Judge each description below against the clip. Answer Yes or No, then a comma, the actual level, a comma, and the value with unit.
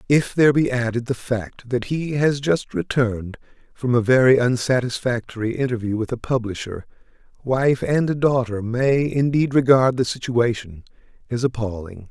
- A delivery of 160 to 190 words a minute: No, average, 145 wpm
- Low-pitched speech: Yes, low, 125 Hz